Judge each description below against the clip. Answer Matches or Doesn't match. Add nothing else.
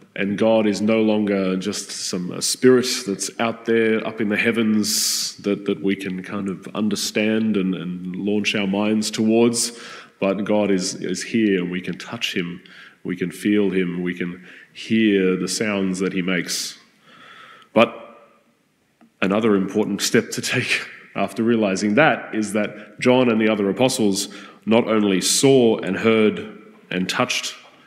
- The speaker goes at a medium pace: Matches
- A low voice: Matches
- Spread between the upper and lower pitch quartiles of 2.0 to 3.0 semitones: Matches